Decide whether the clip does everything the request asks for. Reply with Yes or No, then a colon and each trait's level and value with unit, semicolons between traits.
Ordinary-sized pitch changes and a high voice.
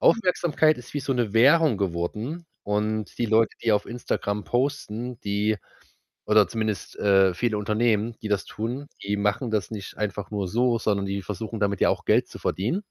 No: average, 3.0 semitones; low, 110 Hz